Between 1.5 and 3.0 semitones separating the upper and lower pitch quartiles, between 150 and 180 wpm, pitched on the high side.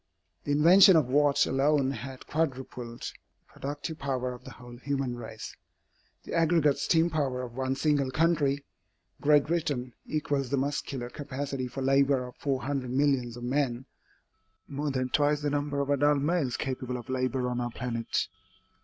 No: narrow, 2.4 semitones; average, 160 wpm; low, 135 Hz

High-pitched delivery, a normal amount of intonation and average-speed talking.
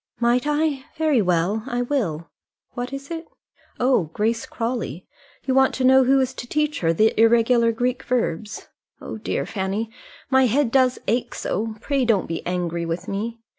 Yes: high, 235 Hz; average, 4.1 semitones; average, 170 wpm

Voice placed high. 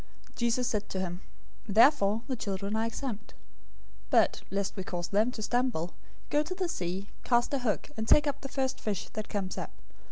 Yes: high, 220 Hz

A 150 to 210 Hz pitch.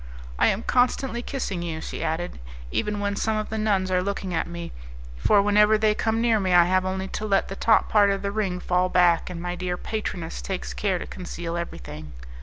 Yes: high, 190 Hz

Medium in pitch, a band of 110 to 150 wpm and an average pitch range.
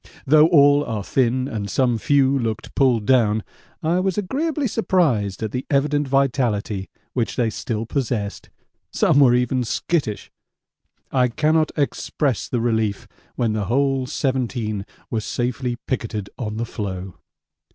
No: low, 125 Hz; average, 140 wpm; average, 4.2 semitones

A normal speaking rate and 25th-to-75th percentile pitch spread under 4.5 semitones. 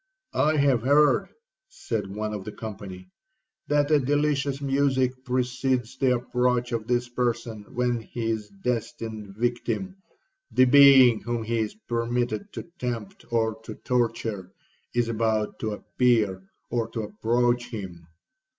No: slow, 125 wpm; average, 2.8 semitones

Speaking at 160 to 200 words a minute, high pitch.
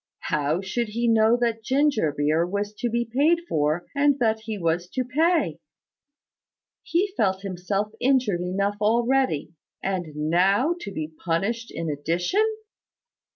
No: average, 145 wpm; high, 210 Hz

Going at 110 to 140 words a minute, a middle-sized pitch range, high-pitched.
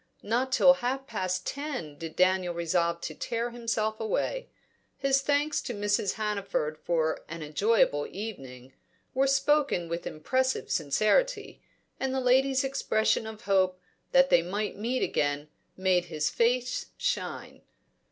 No: slow, 135 wpm; wide, 7.4 semitones; high, 215 Hz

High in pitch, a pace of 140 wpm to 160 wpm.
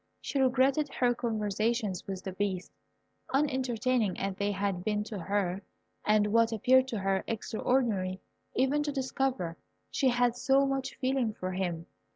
Yes: high, 225 Hz; average, 150 wpm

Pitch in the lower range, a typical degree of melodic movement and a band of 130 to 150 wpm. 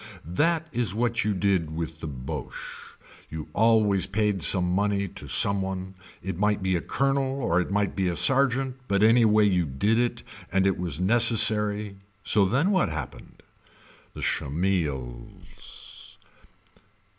Yes: low, 100 Hz; average, 4.2 semitones; average, 145 wpm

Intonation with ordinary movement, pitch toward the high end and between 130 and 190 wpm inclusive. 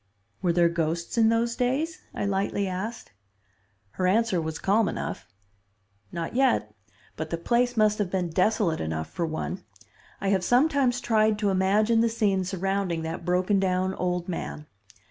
Yes: average, 4.4 semitones; high, 195 Hz; average, 160 wpm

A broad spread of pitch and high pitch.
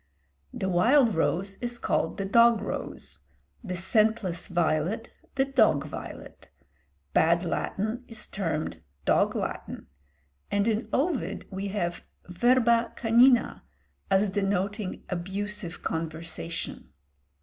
No: average, 4.8 semitones; high, 200 Hz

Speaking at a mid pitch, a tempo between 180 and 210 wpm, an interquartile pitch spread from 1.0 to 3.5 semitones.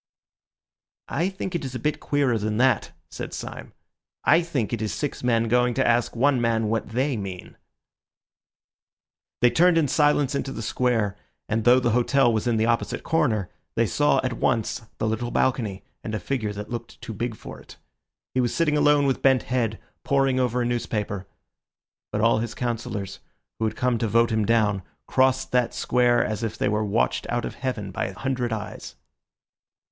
No: low, 120 Hz; average, 190 wpm; average, 3.2 semitones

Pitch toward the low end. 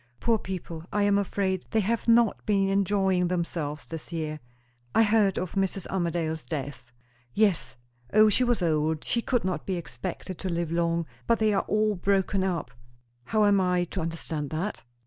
No: medium, 185 Hz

